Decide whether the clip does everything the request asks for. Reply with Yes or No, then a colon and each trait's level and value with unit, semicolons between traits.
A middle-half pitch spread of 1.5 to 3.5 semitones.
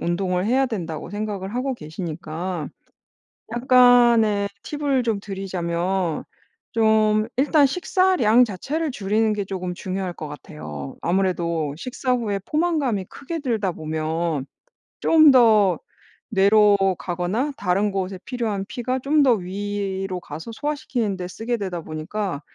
No: wide, 5.4 semitones